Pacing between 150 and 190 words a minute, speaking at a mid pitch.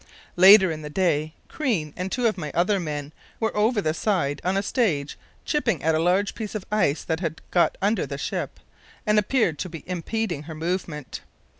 Yes: average, 185 wpm; medium, 180 Hz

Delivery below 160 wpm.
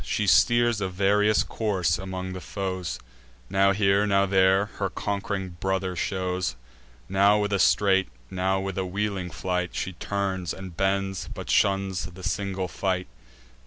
Yes: average, 150 wpm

